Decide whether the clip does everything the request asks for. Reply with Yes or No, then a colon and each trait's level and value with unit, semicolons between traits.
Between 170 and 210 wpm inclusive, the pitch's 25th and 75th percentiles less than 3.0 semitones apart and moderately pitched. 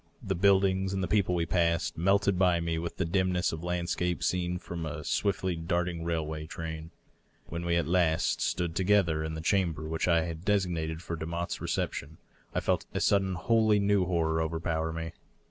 No: average, 185 wpm; narrow, 2.4 semitones; very low, 85 Hz